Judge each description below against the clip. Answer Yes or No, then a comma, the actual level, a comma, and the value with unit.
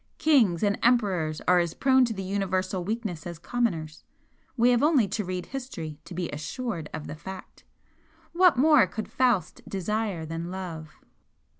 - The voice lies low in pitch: No, high, 190 Hz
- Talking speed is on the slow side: No, average, 160 wpm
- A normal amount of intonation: No, wide, 6.1 semitones